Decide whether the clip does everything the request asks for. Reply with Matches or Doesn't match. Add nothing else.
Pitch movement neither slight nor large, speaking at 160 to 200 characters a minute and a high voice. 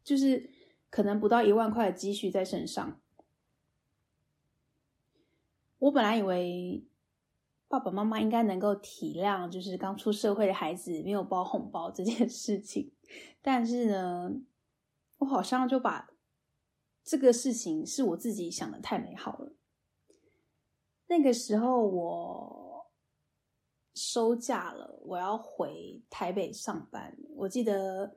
Matches